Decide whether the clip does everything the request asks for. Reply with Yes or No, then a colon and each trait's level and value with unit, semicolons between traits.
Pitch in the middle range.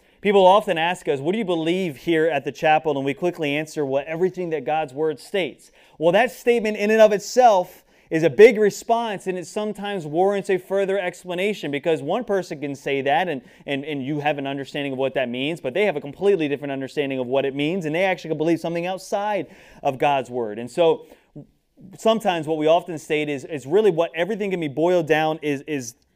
Yes: medium, 165 Hz